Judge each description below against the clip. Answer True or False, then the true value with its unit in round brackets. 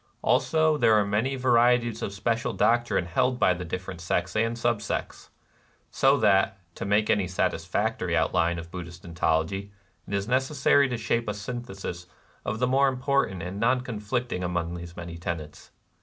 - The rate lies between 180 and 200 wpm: False (170 wpm)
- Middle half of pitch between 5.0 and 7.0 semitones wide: True (5.5 semitones)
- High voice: False (105 Hz)